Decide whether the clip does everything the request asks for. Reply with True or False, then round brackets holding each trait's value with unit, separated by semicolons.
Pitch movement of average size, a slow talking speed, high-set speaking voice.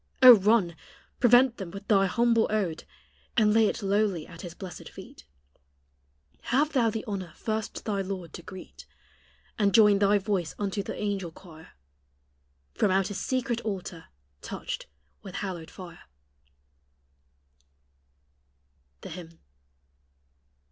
True (3.2 semitones; 125 wpm; 200 Hz)